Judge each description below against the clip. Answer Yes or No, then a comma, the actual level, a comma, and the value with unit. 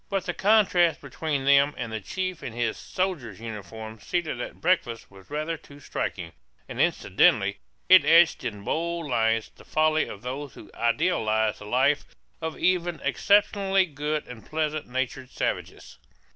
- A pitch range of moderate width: No, wide, 6.5 semitones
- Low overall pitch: No, medium, 145 Hz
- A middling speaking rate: Yes, average, 155 wpm